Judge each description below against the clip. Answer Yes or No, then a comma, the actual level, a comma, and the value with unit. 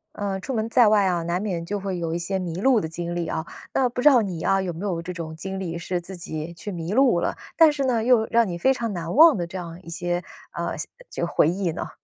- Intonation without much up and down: No, average, 4.3 semitones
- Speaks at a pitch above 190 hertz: No, medium, 185 Hz